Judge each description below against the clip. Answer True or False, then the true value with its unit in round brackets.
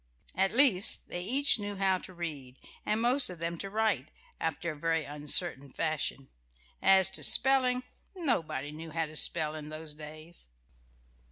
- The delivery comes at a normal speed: True (160 wpm)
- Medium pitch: True (170 Hz)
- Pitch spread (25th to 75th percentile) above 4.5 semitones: True (5.1 semitones)